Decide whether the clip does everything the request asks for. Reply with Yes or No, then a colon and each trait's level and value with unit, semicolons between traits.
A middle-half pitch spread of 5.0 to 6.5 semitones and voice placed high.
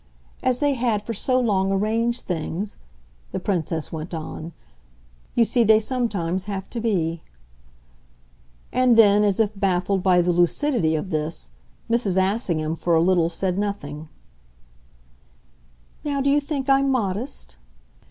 Yes: average, 5.3 semitones; high, 200 Hz